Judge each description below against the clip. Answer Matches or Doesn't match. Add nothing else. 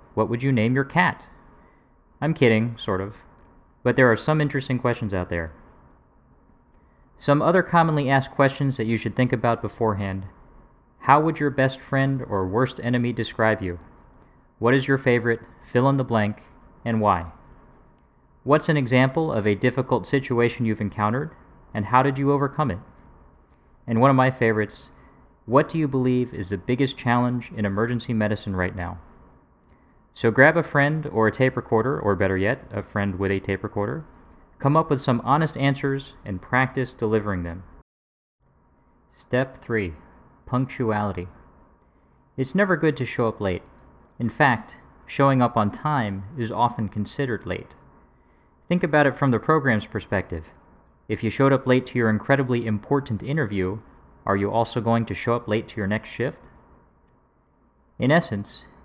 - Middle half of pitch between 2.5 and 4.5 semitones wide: Doesn't match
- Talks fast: Doesn't match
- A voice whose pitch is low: Matches